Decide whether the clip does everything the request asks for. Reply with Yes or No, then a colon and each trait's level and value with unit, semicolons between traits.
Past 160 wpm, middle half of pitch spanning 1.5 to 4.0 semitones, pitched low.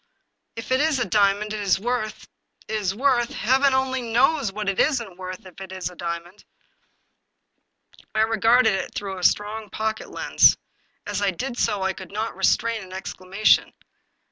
No: average, 180 wpm; average, 3.7 semitones; high, 215 Hz